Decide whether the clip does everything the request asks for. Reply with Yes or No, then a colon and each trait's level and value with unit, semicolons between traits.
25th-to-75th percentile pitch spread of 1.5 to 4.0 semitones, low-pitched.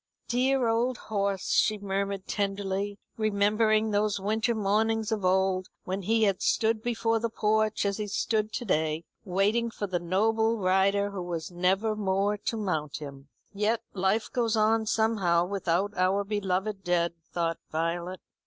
No: average, 2.8 semitones; high, 200 Hz